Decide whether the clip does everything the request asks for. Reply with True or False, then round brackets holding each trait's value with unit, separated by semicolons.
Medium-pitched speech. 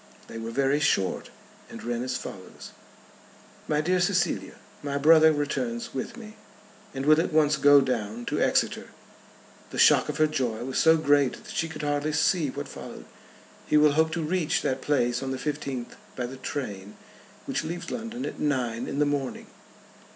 True (145 Hz)